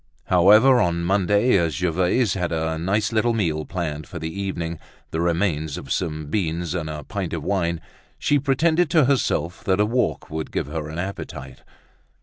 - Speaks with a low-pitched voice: Yes, very low, 85 Hz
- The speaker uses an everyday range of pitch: Yes, average, 4.4 semitones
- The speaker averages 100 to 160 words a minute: No, average, 175 wpm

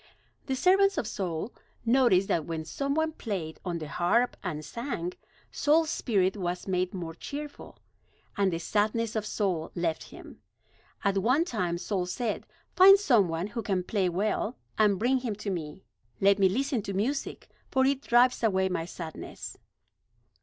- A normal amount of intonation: No, wide, 5.7 semitones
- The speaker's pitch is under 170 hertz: No, high, 200 Hz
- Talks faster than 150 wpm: Yes, average, 165 wpm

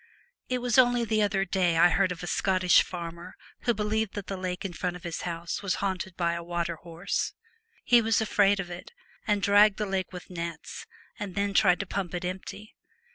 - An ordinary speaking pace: No, fast, 210 wpm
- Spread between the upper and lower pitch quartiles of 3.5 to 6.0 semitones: No, average, 2.7 semitones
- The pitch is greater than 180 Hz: Yes, high, 190 Hz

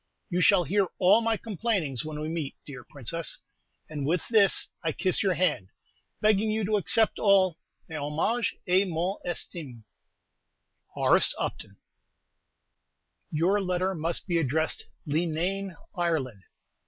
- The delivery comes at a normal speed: No, slow, 130 wpm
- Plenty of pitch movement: No, average, 4.2 semitones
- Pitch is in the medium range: Yes, medium, 175 Hz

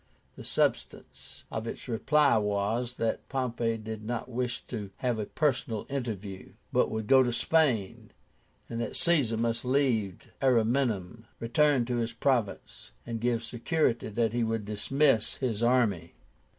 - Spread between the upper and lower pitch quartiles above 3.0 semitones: No, narrow, 2.5 semitones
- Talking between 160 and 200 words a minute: No, slow, 135 wpm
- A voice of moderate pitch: No, low, 115 Hz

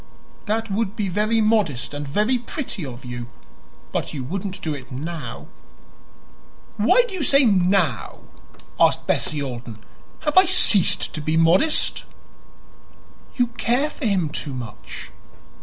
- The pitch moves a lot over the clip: Yes, wide, 7.9 semitones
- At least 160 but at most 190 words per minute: No, average, 140 wpm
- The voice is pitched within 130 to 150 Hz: No, high, 190 Hz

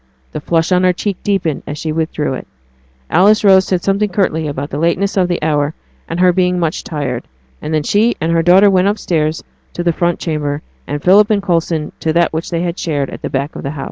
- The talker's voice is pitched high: No, medium, 170 Hz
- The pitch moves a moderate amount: Yes, average, 3.3 semitones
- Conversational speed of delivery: No, fast, 230 wpm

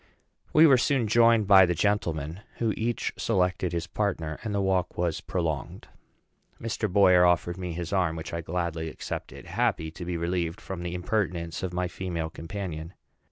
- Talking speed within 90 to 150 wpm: No, average, 170 wpm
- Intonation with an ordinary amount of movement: Yes, average, 3.3 semitones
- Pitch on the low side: Yes, very low, 90 Hz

